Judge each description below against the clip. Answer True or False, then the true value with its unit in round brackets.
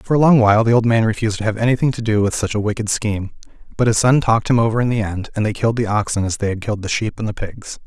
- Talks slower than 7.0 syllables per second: False (7.3 syllables/s)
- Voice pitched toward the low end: True (110 Hz)